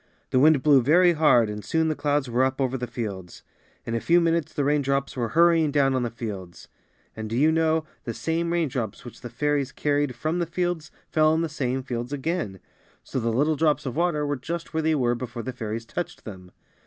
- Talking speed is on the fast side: Yes, fast, 225 wpm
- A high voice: No, medium, 140 Hz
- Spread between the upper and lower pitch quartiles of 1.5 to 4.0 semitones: No, average, 4.9 semitones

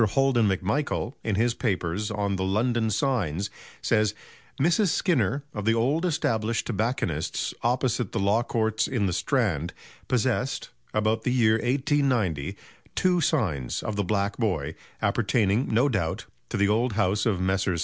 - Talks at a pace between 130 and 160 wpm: Yes, average, 150 wpm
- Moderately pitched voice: No, low, 110 Hz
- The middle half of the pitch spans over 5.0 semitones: No, average, 4.1 semitones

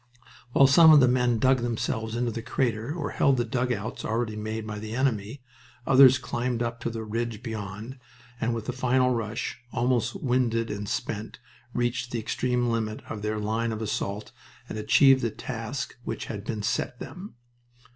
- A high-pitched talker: No, low, 115 Hz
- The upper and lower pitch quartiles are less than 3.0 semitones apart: Yes, narrow, 2.5 semitones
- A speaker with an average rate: Yes, average, 175 wpm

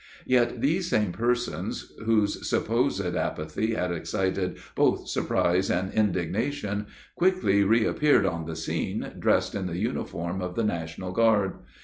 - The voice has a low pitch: Yes, low, 100 Hz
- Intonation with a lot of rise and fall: No, average, 4.2 semitones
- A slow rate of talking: Yes, slow, 130 wpm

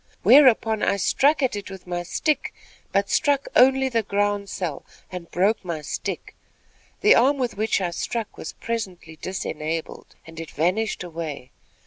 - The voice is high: Yes, high, 200 Hz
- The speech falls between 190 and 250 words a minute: No, average, 155 wpm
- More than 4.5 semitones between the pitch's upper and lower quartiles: Yes, average, 5.2 semitones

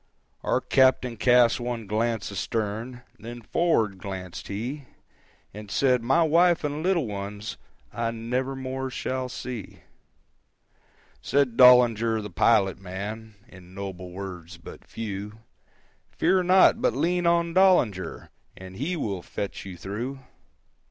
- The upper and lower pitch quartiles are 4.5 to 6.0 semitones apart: Yes, average, 5.0 semitones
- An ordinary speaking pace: No, slow, 125 wpm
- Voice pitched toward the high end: No, low, 115 Hz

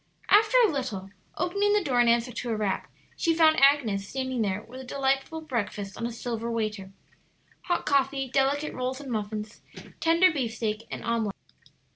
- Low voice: No, very high, 250 Hz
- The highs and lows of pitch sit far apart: No, average, 4.6 semitones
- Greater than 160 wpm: Yes, average, 170 wpm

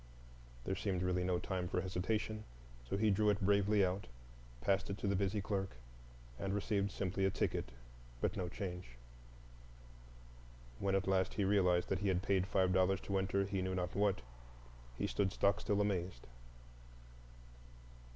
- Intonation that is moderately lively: No, narrow, 1.5 semitones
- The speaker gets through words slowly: No, average, 160 wpm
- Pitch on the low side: Yes, very low, 95 Hz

